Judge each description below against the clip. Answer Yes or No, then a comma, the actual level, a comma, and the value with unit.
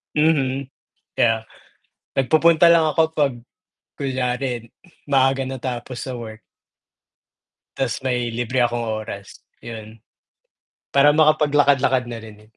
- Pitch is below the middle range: Yes, low, 130 Hz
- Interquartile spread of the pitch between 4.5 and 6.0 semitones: No, average, 3.2 semitones